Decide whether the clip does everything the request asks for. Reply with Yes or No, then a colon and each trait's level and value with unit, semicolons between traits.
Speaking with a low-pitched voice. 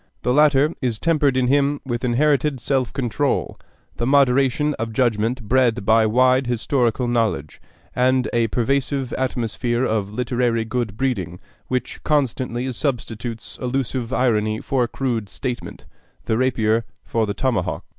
Yes: low, 125 Hz